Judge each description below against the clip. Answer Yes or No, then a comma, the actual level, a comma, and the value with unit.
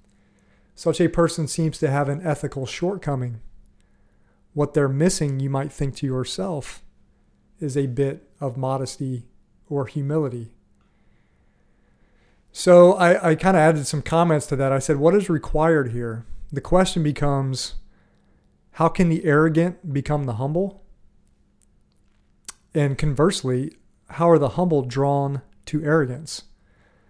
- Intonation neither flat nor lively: Yes, average, 3.6 semitones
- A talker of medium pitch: Yes, medium, 145 Hz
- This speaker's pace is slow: Yes, slow, 130 wpm